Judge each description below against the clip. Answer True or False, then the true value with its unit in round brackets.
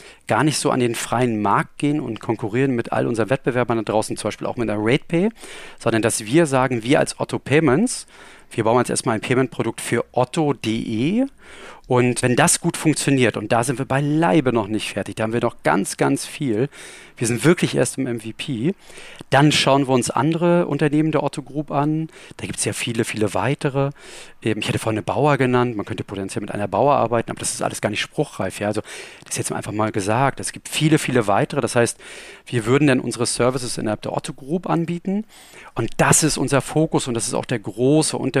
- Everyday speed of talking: False (215 wpm)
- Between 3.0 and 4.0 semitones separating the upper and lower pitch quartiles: False (4.6 semitones)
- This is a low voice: True (130 Hz)